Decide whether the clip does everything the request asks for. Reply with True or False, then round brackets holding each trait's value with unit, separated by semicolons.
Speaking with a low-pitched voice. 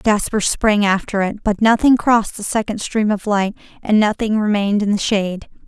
False (210 Hz)